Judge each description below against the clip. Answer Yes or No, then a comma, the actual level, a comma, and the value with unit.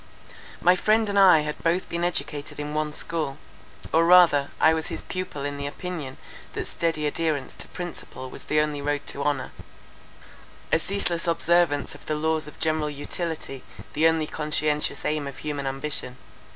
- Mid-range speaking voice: Yes, medium, 155 Hz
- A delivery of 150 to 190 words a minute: Yes, average, 170 wpm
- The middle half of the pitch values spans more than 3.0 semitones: No, narrow, 2.5 semitones